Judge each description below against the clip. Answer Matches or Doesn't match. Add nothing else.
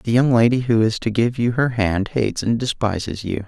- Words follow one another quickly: Matches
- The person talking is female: Doesn't match